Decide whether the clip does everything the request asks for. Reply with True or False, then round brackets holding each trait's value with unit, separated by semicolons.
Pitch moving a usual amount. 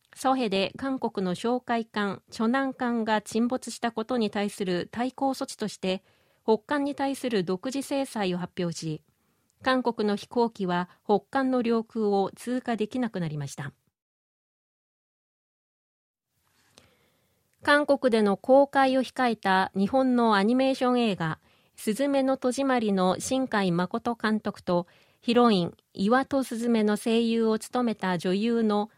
True (4.4 semitones)